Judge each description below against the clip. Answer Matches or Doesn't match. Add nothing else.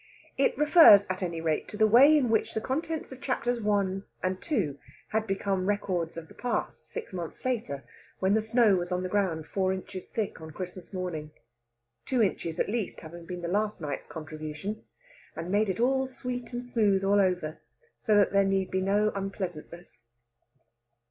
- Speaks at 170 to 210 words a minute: Matches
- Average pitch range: Matches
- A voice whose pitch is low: Doesn't match